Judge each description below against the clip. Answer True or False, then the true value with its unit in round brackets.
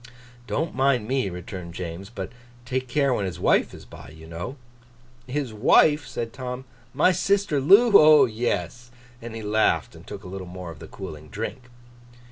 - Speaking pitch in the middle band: False (115 Hz)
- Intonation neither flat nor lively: False (6.8 semitones)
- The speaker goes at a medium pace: True (175 wpm)